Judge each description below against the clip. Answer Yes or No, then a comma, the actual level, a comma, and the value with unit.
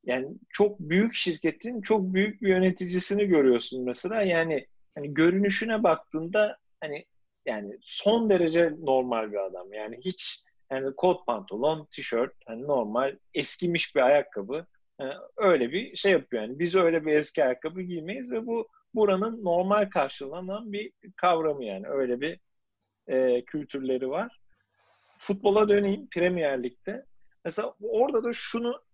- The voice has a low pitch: No, medium, 180 Hz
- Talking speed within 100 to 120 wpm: No, average, 135 wpm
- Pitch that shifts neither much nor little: No, wide, 6.7 semitones